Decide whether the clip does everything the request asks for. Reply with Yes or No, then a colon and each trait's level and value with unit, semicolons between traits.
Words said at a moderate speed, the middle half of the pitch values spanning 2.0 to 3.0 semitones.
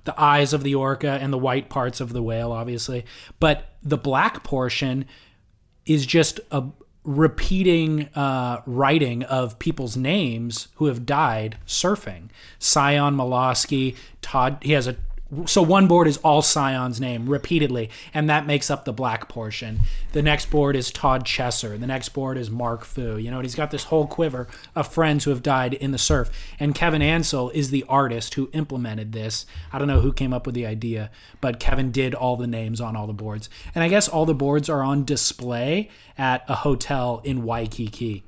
No: average, 190 wpm; average, 3.9 semitones